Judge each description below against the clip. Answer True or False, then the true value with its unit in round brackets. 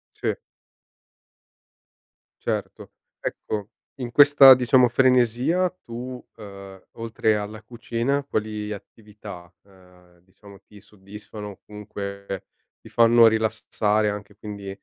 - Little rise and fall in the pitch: False (3.0 semitones)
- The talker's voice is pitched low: True (105 Hz)